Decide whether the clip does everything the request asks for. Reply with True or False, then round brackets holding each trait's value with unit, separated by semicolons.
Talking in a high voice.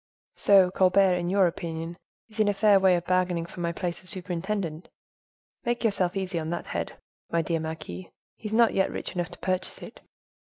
False (180 Hz)